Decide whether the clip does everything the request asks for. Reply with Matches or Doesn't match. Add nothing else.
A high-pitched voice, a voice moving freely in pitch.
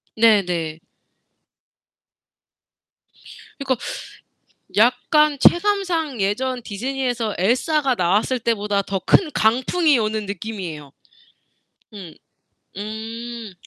Doesn't match